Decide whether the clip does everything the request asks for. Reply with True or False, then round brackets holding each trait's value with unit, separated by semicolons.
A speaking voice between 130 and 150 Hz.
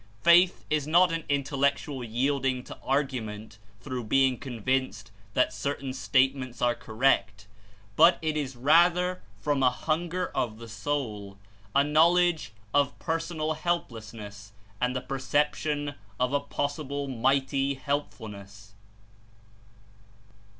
True (135 Hz)